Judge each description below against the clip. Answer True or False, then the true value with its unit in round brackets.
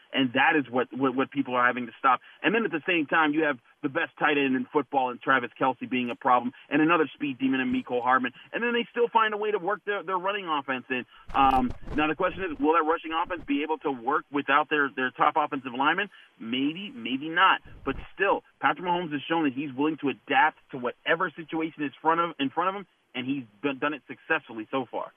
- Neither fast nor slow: False (245 wpm)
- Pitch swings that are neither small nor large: False (5.9 semitones)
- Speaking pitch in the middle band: True (150 Hz)